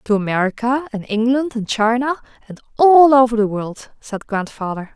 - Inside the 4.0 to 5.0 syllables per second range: Yes, 4.9 syllables/s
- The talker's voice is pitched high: Yes, high, 235 Hz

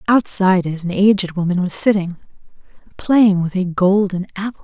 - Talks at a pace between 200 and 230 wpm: No, average, 155 wpm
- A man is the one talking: No, female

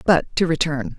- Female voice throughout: Yes, female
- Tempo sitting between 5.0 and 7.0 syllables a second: No, 4.6 syllables/s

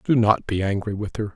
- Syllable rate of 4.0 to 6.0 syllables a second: Yes, 5.6 syllables/s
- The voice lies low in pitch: Yes, low, 105 Hz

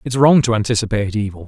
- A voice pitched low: Yes, low, 110 Hz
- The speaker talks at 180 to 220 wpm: Yes, fast, 205 wpm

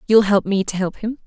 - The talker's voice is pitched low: No, high, 205 Hz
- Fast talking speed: Yes, fast, 285 wpm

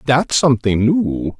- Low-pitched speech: Yes, low, 130 Hz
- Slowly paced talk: Yes, slow, 130 wpm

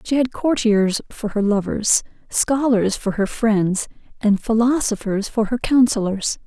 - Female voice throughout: Yes, female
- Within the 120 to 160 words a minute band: Yes, average, 140 wpm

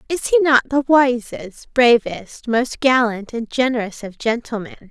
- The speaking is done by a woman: Yes, female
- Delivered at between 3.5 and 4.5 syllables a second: Yes, 4.3 syllables/s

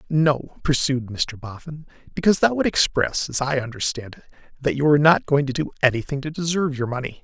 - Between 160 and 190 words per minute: No, average, 200 wpm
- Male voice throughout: Yes, male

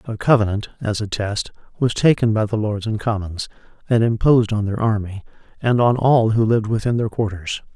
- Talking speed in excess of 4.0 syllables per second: Yes, 5.5 syllables/s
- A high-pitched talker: No, low, 110 Hz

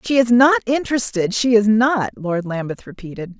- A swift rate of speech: No, average, 160 wpm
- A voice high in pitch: Yes, high, 220 Hz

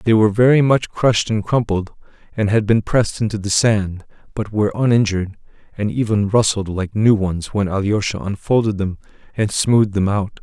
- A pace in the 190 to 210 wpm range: No, average, 180 wpm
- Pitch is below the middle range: Yes, low, 105 Hz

